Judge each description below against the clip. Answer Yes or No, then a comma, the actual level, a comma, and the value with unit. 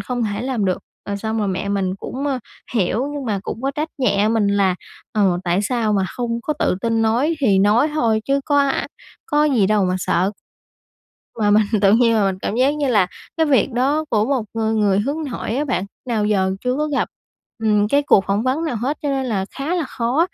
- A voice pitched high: Yes, high, 225 Hz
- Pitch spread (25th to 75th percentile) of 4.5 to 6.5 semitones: Yes, average, 5.1 semitones